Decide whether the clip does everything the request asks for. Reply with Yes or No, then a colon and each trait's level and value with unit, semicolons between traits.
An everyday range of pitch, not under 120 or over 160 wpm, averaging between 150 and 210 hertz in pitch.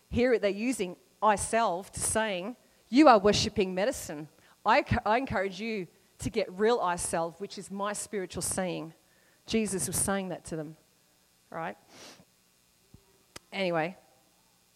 Yes: average, 4.8 semitones; average, 140 wpm; high, 190 Hz